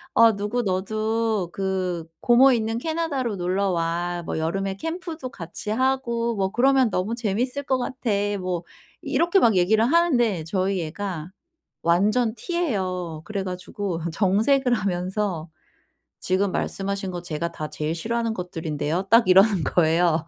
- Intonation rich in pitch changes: No, average, 5.0 semitones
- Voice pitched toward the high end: Yes, high, 200 Hz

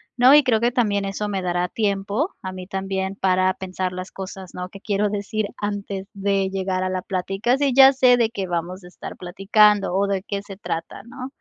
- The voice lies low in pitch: No, high, 195 Hz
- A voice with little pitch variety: Yes, narrow, 2.1 semitones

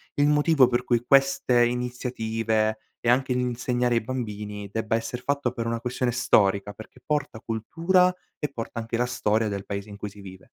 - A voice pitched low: Yes, low, 120 Hz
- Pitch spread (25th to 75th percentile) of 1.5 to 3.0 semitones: Yes, narrow, 2.6 semitones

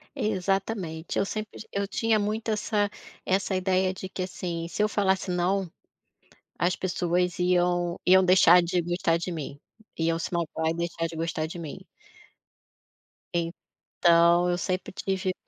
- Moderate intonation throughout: No, narrow, 2.1 semitones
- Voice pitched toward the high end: No, medium, 180 Hz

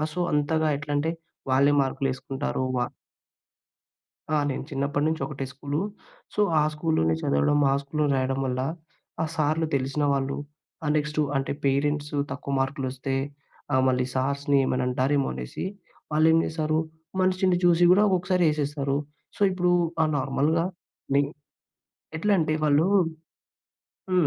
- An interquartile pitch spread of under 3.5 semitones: Yes, average, 2.8 semitones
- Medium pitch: Yes, medium, 145 Hz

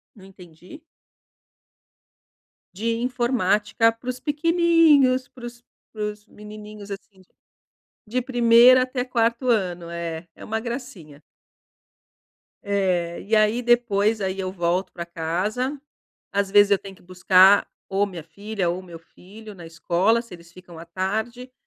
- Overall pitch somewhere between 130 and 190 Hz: No, high, 210 Hz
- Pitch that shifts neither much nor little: Yes, average, 4.7 semitones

